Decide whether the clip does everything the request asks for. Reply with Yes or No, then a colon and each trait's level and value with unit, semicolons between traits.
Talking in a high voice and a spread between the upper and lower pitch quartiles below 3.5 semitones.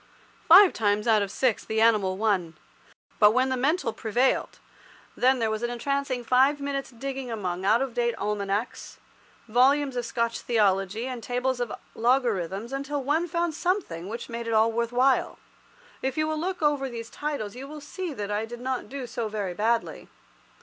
No: high, 240 Hz; average, 3.9 semitones